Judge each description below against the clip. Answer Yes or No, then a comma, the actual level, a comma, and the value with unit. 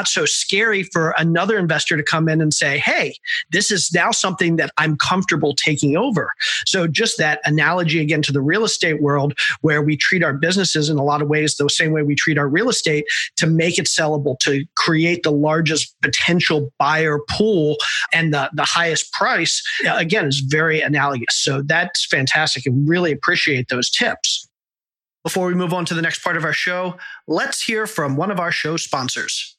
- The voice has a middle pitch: Yes, medium, 160 Hz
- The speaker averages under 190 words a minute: No, average, 195 wpm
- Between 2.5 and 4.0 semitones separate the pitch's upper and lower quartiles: Yes, average, 2.8 semitones